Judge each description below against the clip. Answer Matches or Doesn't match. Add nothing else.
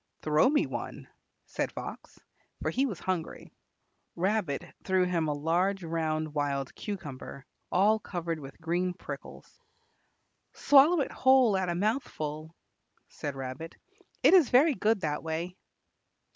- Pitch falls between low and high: Matches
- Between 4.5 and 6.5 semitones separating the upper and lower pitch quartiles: Matches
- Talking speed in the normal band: Doesn't match